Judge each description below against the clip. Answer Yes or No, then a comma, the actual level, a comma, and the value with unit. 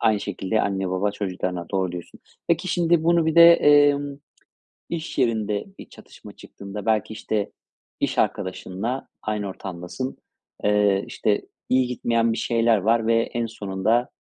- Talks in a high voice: No, low, 110 Hz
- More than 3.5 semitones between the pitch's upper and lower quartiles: Yes, average, 4.8 semitones